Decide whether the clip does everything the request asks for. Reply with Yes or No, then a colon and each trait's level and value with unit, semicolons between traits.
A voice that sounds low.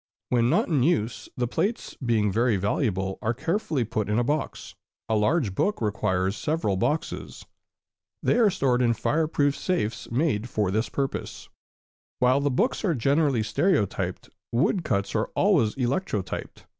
Yes: low, 120 Hz